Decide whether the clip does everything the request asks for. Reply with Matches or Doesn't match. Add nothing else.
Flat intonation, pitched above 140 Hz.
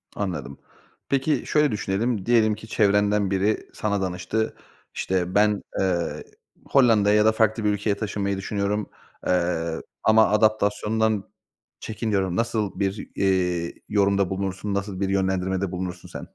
Doesn't match